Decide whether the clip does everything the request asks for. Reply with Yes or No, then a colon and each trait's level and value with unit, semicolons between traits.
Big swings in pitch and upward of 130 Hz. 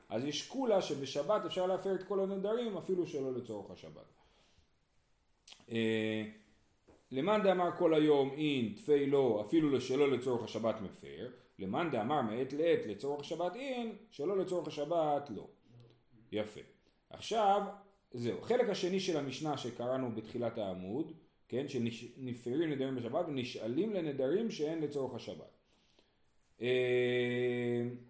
Yes: wide, 7.4 semitones; medium, 140 Hz